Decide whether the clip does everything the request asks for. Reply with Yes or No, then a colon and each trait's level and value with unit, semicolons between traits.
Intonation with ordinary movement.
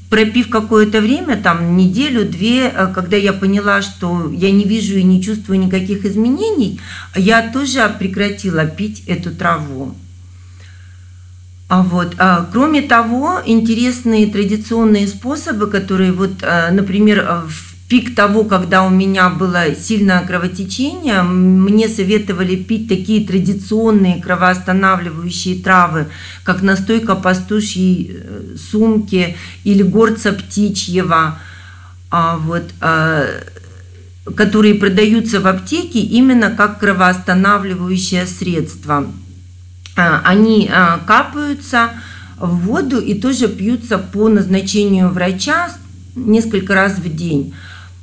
Yes: average, 3.6 semitones